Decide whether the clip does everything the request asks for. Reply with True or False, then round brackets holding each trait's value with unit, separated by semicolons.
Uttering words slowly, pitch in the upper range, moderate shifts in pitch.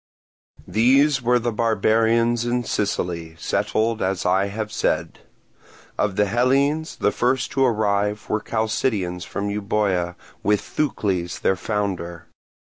False (125 wpm; 105 Hz; 3.4 semitones)